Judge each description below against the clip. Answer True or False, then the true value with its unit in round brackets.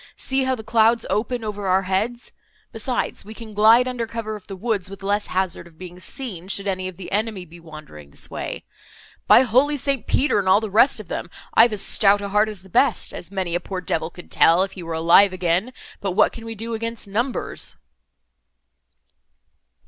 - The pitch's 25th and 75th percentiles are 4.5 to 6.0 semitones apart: False (3.7 semitones)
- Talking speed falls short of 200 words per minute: False (205 wpm)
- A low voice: False (205 Hz)